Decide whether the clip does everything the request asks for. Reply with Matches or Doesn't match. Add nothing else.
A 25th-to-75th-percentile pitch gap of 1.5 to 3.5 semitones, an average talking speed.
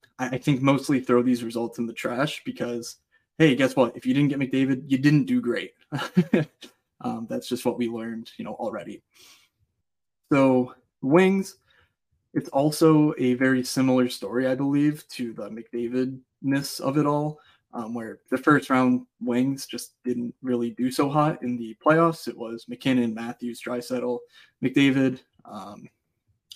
Matches